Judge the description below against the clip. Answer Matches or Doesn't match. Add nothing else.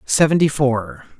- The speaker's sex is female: Doesn't match